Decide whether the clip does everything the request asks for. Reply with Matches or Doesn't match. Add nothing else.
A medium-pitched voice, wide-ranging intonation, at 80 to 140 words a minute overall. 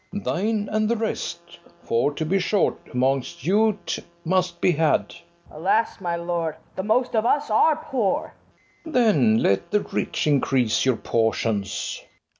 Doesn't match